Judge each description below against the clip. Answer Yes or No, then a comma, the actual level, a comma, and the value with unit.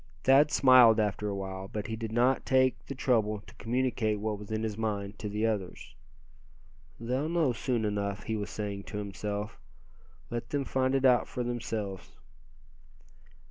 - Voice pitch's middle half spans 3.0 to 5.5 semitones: Yes, average, 3.4 semitones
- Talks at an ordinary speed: Yes, average, 170 wpm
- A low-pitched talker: Yes, low, 110 Hz